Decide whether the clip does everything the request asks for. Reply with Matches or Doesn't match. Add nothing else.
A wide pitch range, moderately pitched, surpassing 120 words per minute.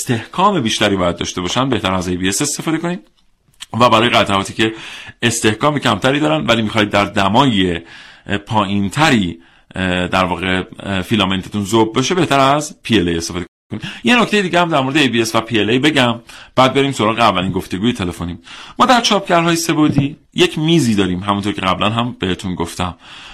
Doesn't match